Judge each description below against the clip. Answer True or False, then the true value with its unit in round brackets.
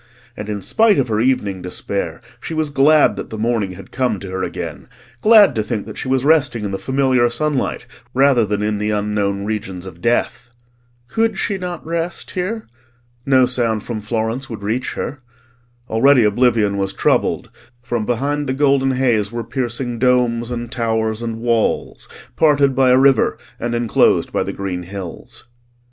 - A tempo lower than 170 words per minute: False (175 wpm)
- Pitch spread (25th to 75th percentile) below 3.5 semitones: False (4.1 semitones)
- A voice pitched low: True (120 Hz)